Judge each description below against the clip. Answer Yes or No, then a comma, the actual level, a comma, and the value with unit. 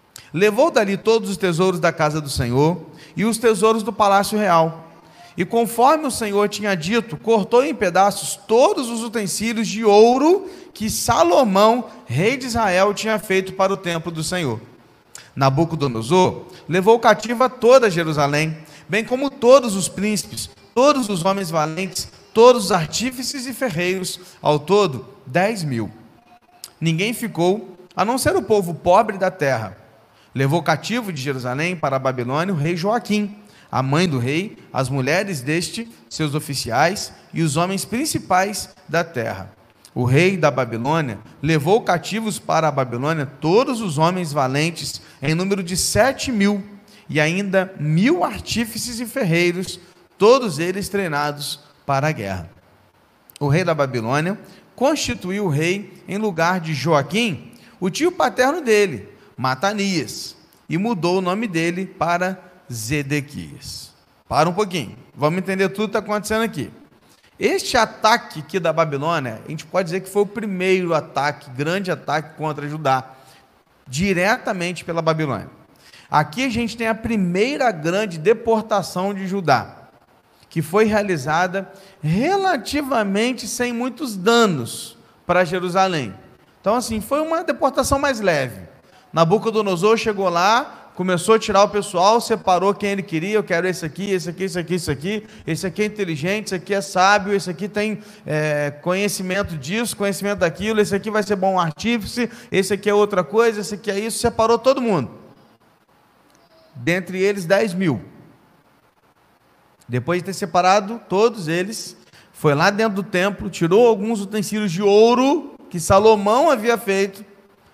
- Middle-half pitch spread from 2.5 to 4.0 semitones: No, average, 5.2 semitones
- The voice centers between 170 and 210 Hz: Yes, high, 190 Hz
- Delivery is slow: No, average, 150 wpm